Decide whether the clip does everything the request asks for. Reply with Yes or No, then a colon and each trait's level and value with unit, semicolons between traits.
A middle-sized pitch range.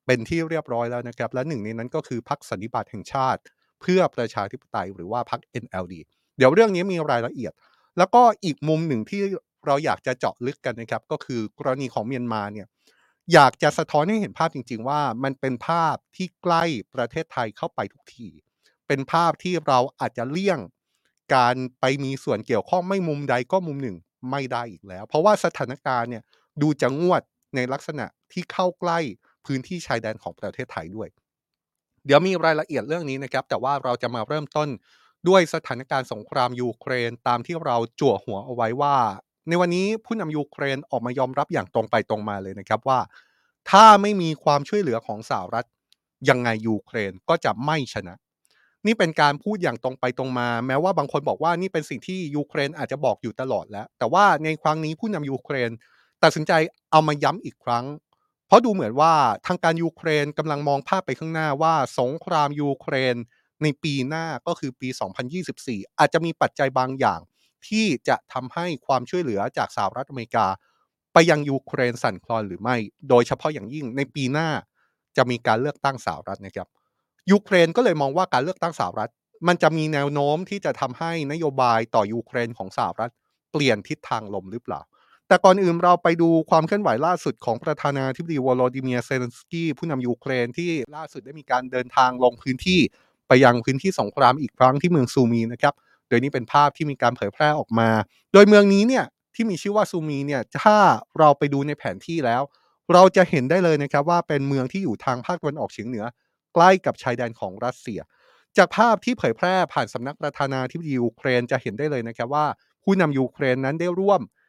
Yes: average, 5.0 semitones